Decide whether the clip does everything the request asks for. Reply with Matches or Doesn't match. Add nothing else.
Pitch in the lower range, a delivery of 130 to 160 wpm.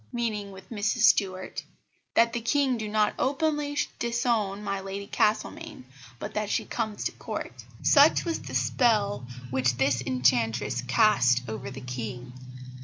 Doesn't match